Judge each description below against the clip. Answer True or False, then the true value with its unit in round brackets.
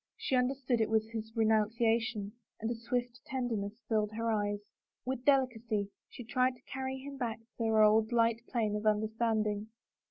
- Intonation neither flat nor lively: False (2.3 semitones)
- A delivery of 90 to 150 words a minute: False (165 wpm)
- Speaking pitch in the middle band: False (225 Hz)